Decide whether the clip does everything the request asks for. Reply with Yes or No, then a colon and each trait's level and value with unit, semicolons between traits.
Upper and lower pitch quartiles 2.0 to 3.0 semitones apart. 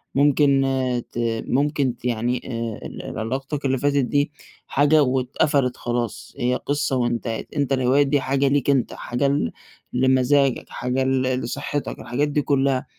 Yes: narrow, 2.4 semitones